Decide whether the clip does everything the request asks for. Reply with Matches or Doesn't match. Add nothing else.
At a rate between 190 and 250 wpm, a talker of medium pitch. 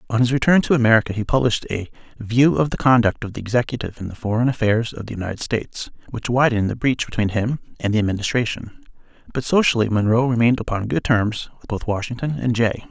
Doesn't match